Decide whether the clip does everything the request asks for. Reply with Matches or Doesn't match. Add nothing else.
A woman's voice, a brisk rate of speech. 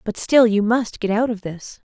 Matches